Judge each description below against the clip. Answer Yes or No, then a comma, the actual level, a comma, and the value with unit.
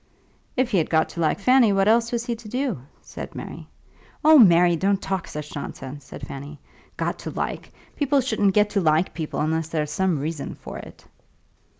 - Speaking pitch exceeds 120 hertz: Yes, medium, 185 Hz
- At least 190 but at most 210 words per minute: Yes, average, 195 wpm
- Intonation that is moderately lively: No, wide, 6.8 semitones